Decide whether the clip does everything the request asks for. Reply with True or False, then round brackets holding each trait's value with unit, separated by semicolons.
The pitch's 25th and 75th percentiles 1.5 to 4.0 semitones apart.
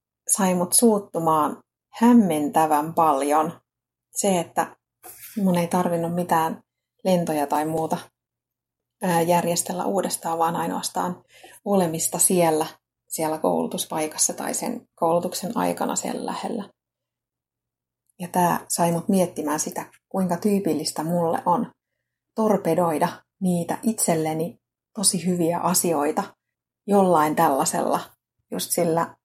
True (2.6 semitones)